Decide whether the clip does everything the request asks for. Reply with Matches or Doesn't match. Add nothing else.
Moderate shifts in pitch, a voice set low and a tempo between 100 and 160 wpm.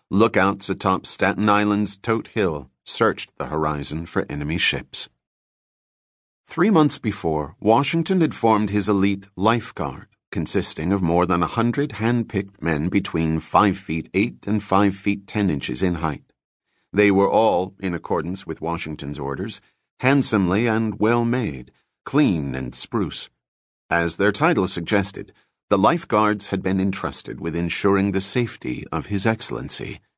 Matches